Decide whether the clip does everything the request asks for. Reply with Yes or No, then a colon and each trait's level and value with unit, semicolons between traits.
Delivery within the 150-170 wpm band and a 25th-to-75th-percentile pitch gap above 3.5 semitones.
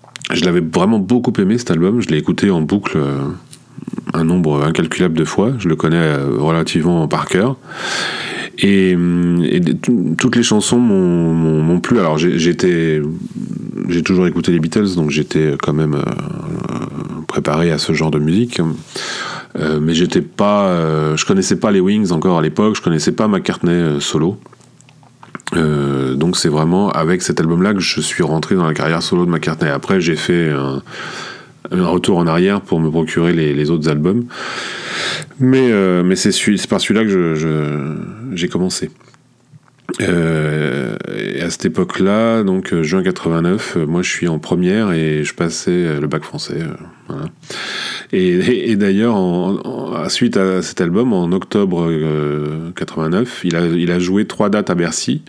Yes: average, 165 wpm; average, 4.2 semitones